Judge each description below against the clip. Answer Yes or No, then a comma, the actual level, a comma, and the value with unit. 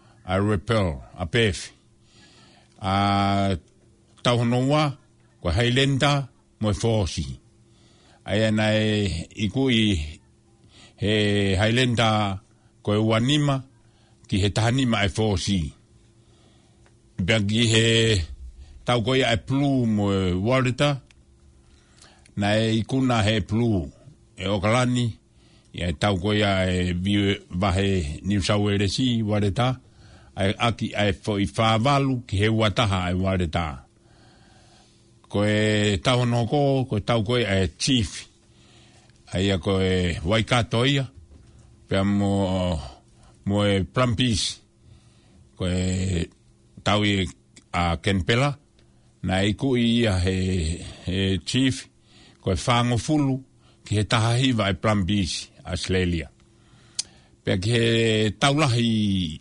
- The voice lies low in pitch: Yes, low, 110 Hz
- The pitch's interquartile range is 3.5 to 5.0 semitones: No, average, 3.1 semitones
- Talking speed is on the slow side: Yes, slow, 100 wpm